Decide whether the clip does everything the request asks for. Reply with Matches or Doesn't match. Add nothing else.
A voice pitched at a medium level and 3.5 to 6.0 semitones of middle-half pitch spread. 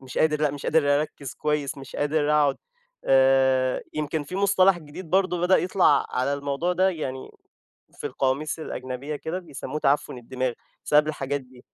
Doesn't match